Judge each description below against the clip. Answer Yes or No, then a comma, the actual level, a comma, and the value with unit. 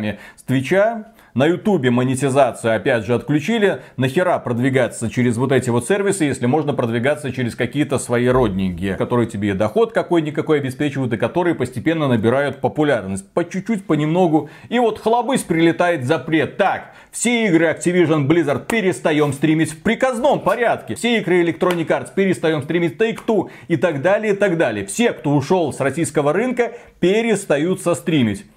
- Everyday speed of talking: Yes, average, 150 wpm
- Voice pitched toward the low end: No, medium, 160 Hz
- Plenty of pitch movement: Yes, wide, 6.3 semitones